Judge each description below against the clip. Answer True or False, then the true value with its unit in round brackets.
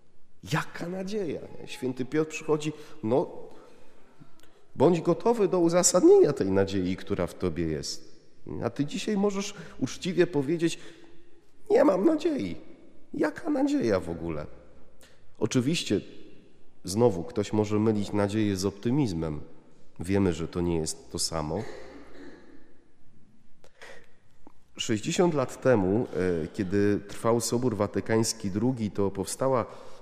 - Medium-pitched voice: False (120 Hz)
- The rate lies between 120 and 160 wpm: False (110 wpm)